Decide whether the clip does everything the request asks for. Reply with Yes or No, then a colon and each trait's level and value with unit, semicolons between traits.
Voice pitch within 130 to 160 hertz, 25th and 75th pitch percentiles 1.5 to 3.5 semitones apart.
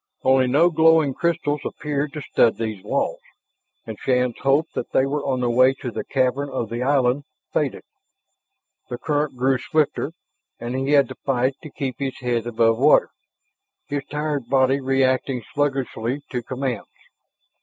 Yes: low, 135 Hz; narrow, 2.5 semitones